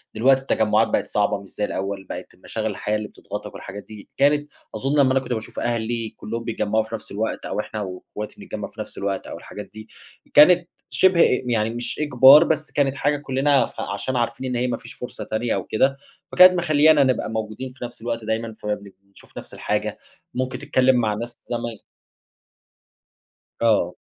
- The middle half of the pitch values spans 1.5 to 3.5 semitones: No, average, 3.9 semitones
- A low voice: Yes, low, 120 Hz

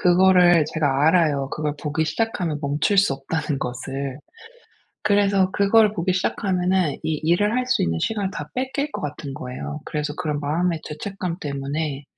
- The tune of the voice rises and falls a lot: No, average, 4.6 semitones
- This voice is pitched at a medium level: Yes, medium, 160 Hz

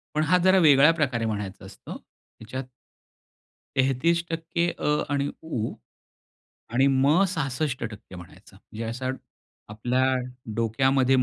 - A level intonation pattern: No, average, 4.9 semitones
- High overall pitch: No, low, 130 Hz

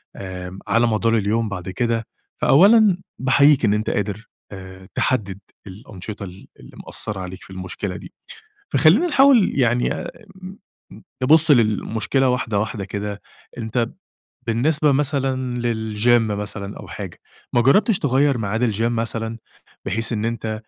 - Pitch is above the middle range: No, low, 115 Hz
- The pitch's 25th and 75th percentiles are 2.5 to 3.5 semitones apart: No, average, 4.2 semitones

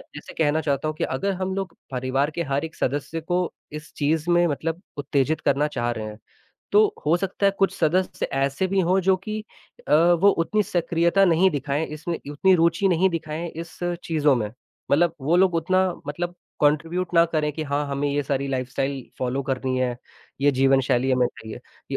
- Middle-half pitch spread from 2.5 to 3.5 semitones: No, average, 4.0 semitones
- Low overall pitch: No, medium, 155 Hz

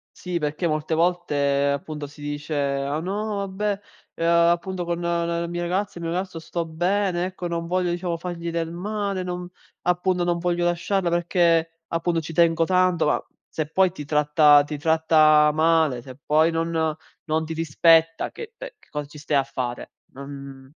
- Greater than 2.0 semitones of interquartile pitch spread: Yes, narrow, 2.6 semitones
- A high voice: No, medium, 165 Hz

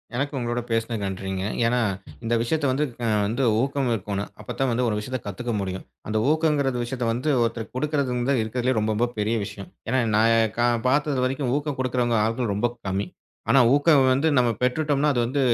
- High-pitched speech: No, low, 125 Hz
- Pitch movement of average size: Yes, average, 3.4 semitones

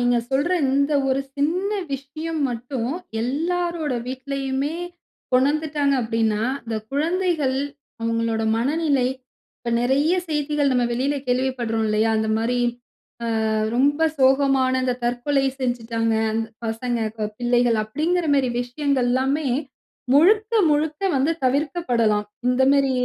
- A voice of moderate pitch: No, very high, 265 Hz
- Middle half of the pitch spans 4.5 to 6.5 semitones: No, average, 3.5 semitones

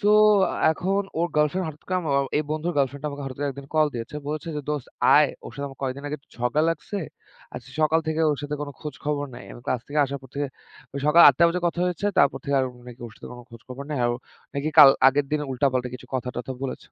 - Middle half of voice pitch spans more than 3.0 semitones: No, narrow, 2.6 semitones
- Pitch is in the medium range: Yes, medium, 145 Hz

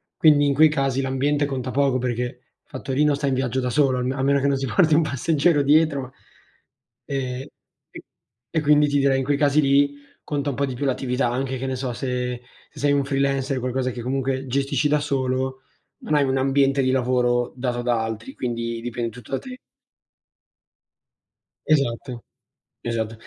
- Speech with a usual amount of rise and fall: No, narrow, 2.1 semitones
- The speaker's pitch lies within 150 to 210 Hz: No, low, 135 Hz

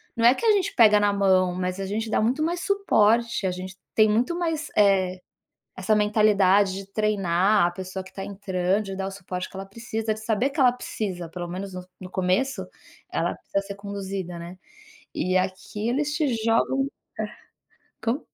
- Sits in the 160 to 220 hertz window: Yes, high, 200 Hz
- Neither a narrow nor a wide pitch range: Yes, average, 3.4 semitones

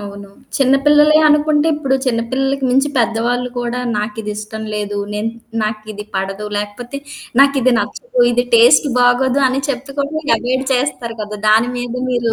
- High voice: Yes, high, 245 Hz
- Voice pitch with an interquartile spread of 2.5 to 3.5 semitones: No, average, 4.0 semitones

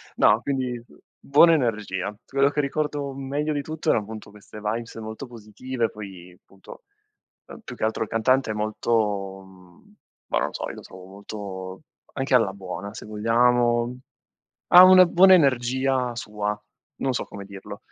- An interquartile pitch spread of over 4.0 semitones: Yes, average, 4.6 semitones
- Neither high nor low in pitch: No, low, 115 Hz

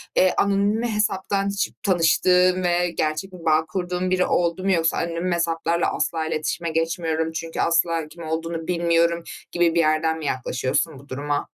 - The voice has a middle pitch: Yes, medium, 170 Hz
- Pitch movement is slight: Yes, narrow, 2.1 semitones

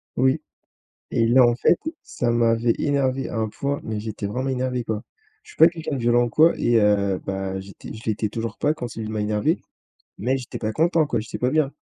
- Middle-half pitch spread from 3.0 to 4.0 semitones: Yes, average, 3.5 semitones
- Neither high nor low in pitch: No, low, 120 Hz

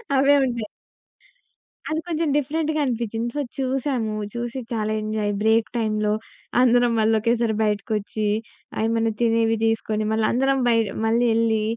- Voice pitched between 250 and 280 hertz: No, high, 230 Hz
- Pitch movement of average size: No, narrow, 2.3 semitones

